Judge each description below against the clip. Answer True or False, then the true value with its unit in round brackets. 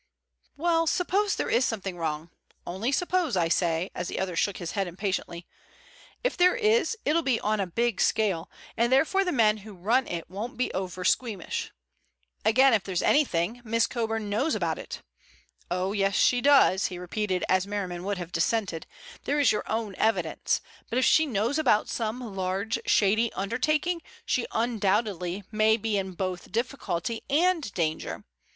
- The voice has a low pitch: False (215 Hz)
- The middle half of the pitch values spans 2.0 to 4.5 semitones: False (5.3 semitones)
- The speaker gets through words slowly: False (165 wpm)